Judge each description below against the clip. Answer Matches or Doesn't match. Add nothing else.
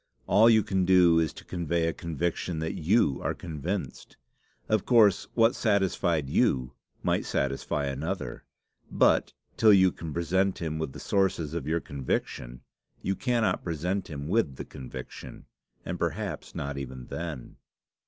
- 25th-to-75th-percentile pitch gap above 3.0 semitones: Matches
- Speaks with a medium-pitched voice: Doesn't match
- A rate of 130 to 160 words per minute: Matches